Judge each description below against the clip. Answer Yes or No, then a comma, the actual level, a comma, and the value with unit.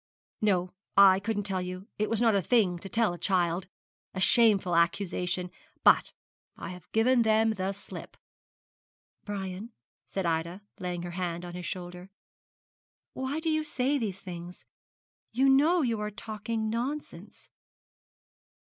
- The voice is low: No, high, 200 Hz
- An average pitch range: Yes, average, 4.1 semitones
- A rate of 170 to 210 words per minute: No, average, 145 wpm